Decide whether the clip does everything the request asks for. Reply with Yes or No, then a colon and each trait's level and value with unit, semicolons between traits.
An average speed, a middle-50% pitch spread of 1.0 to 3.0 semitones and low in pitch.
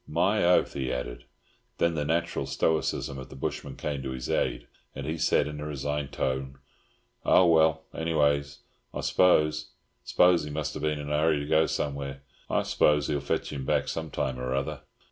Yes: average, 185 wpm; narrow, 2.4 semitones; very low, 75 Hz